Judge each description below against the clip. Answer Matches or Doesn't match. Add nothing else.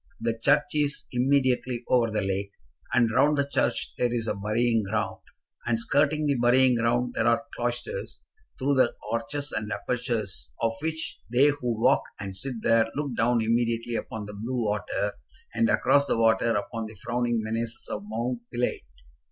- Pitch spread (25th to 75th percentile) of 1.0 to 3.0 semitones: Matches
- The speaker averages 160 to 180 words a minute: Matches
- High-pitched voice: Doesn't match